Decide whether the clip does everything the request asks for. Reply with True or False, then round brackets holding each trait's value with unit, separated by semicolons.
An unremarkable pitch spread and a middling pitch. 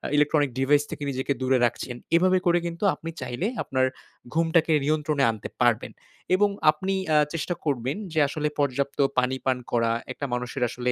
True (3.9 semitones; 145 Hz)